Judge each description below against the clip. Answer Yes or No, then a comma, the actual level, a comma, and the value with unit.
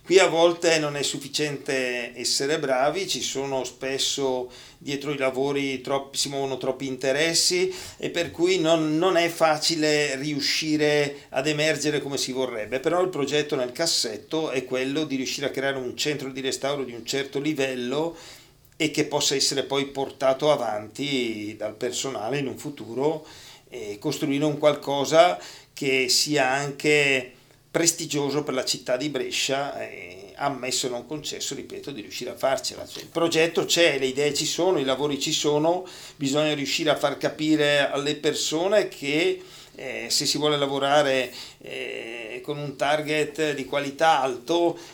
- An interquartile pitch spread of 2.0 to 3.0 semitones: Yes, narrow, 2.5 semitones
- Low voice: No, medium, 145 Hz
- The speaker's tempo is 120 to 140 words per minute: No, average, 160 wpm